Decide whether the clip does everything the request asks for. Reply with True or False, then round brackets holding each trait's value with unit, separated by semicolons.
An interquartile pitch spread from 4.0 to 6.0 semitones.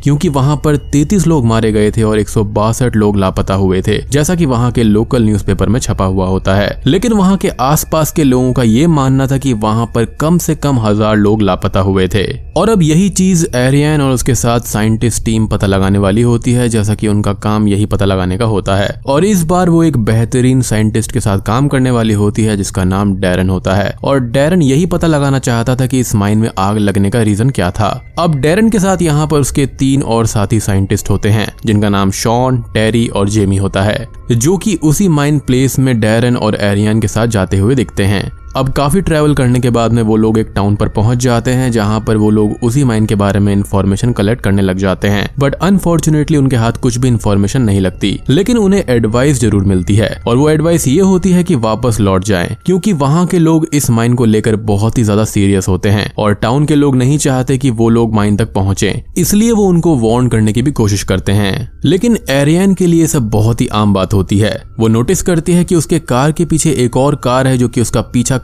True (5.4 semitones)